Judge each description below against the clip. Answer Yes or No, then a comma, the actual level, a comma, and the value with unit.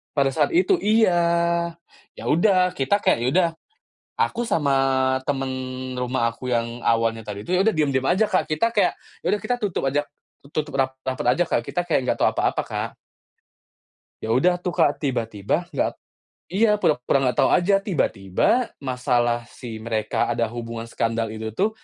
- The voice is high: No, medium, 140 Hz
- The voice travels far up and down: Yes, wide, 7.4 semitones